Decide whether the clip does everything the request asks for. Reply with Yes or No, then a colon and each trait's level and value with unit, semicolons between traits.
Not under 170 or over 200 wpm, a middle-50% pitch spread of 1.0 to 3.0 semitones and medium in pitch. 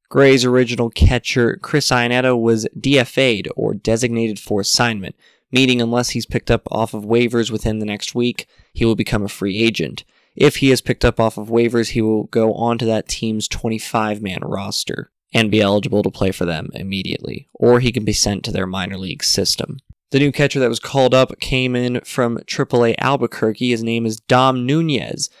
No: average, 190 wpm; average, 2.7 semitones; low, 115 Hz